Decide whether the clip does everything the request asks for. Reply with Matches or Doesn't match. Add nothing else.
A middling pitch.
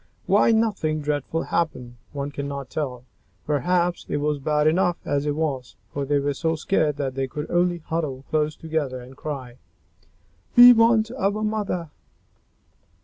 Matches